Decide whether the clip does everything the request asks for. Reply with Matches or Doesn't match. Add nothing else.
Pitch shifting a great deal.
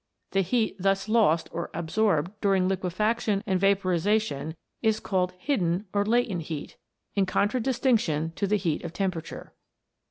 Doesn't match